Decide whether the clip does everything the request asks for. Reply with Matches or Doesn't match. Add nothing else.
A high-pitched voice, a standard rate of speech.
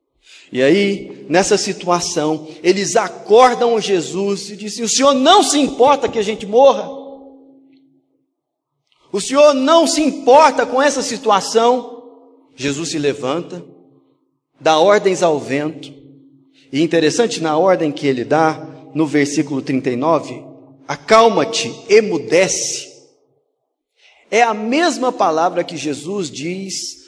Doesn't match